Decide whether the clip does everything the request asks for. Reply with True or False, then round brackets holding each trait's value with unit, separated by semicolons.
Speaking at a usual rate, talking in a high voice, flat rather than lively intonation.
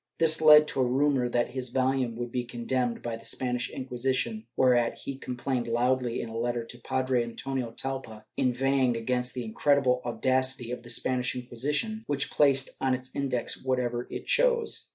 False (175 wpm; 125 Hz; 1.8 semitones)